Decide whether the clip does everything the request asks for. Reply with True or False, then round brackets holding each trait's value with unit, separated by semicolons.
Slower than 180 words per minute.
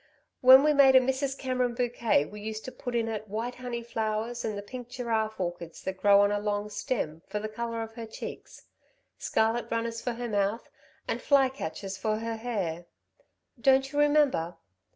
False (190 wpm)